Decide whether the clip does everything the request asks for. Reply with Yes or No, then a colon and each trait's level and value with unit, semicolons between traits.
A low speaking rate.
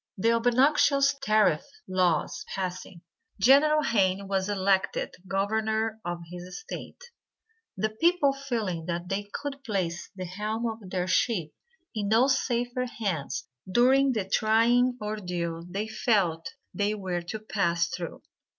Yes: slow, 130 wpm